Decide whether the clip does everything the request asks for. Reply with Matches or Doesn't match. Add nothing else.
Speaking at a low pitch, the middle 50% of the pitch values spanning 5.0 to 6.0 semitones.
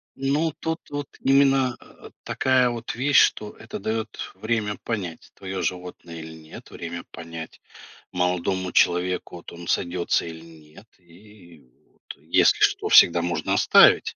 Matches